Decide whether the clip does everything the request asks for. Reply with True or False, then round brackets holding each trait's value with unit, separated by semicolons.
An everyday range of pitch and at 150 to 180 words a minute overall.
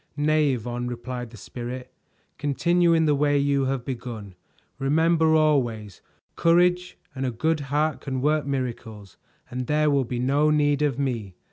True (3.7 semitones; 155 wpm)